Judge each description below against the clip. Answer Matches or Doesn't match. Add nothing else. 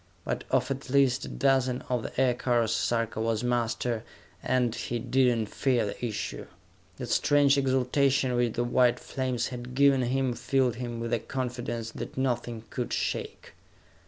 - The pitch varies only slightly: Matches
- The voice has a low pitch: Matches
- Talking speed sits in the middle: Matches